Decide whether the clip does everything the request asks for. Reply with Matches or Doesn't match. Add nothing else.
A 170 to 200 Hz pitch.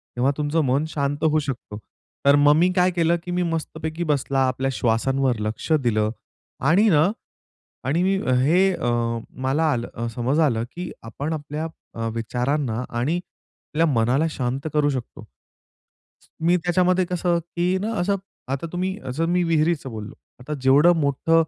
Doesn't match